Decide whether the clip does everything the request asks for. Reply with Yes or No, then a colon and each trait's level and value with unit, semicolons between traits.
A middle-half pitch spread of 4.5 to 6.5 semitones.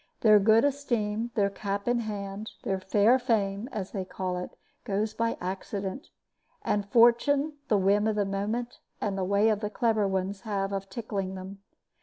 No: narrow, 2.6 semitones